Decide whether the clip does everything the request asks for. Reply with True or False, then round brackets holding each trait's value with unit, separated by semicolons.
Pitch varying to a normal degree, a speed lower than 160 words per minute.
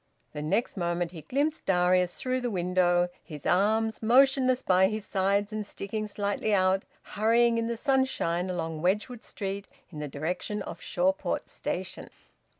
True (4.0 semitones; 150 wpm)